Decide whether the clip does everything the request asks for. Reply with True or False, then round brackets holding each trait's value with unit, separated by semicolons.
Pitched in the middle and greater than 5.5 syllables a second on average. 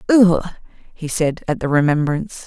False (165 Hz; 5.0 syllables/s)